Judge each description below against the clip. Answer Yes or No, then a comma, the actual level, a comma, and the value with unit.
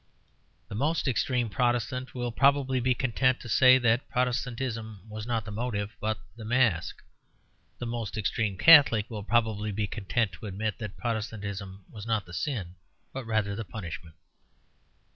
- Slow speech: No, average, 155 wpm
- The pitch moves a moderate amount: Yes, average, 3.2 semitones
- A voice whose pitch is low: Yes, low, 110 Hz